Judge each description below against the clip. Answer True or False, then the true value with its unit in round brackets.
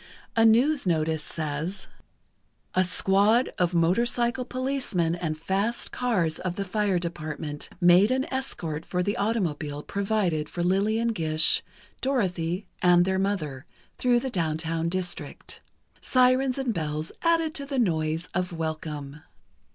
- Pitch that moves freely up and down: True (6.2 semitones)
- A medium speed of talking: False (130 wpm)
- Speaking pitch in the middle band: True (180 Hz)